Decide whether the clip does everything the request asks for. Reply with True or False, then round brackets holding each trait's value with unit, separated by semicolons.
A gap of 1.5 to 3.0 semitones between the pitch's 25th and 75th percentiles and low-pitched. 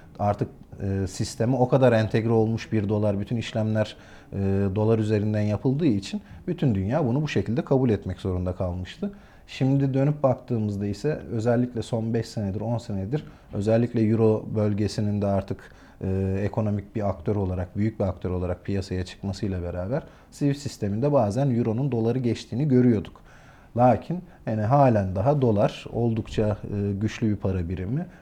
False (3.7 semitones; 110 Hz)